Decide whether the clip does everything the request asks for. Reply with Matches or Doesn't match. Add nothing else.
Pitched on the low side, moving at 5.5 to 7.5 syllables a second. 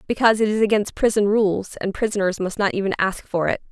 Doesn't match